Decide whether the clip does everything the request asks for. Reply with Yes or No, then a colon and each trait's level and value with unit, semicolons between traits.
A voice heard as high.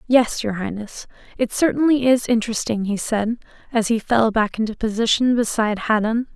Yes: high, 225 Hz